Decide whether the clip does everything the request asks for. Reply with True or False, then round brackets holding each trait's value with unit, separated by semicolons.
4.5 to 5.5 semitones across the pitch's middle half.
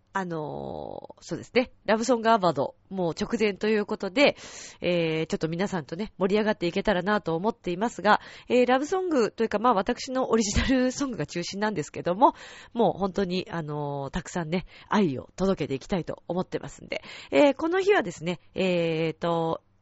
True (5.2 semitones)